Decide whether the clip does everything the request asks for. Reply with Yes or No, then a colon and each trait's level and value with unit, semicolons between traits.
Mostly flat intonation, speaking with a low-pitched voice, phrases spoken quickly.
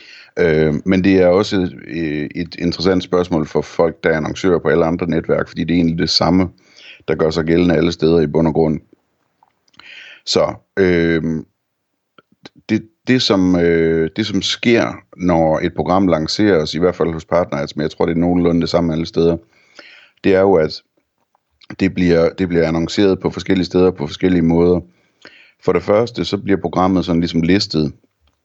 No: narrow, 2.2 semitones; very low, 85 Hz; average, 180 wpm